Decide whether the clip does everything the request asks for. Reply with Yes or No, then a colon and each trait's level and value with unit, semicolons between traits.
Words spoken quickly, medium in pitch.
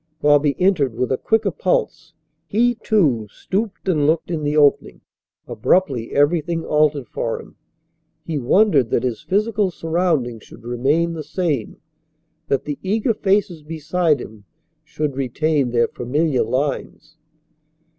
No: slow, 135 wpm; medium, 155 Hz